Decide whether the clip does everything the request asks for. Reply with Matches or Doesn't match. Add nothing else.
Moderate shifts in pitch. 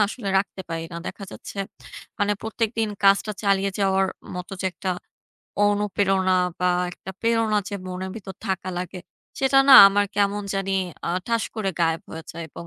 Doesn't match